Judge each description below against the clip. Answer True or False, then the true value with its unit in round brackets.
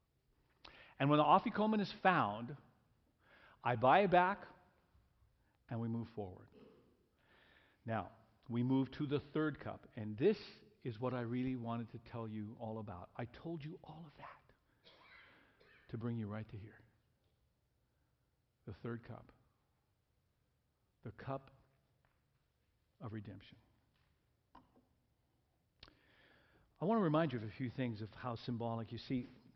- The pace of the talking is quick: False (135 wpm)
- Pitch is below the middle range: True (120 Hz)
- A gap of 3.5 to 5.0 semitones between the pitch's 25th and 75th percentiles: True (4.1 semitones)